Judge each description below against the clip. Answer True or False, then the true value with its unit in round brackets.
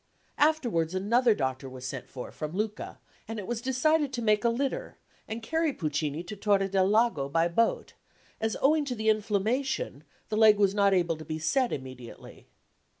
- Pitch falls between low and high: False (210 Hz)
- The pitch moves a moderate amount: False (6.5 semitones)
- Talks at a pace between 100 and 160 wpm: False (180 wpm)